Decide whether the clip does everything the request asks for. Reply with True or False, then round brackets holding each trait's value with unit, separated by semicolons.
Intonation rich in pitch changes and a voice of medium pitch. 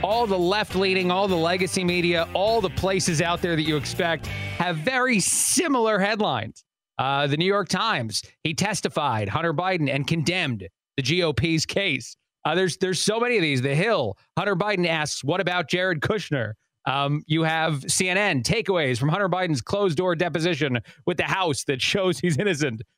False (4.1 semitones; 175 Hz)